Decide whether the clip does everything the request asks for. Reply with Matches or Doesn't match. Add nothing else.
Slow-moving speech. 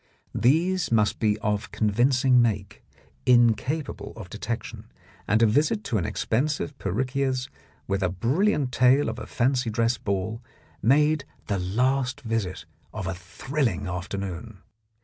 Matches